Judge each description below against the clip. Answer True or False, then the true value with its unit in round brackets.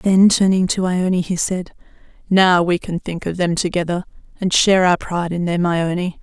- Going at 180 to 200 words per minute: True (195 wpm)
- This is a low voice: False (180 Hz)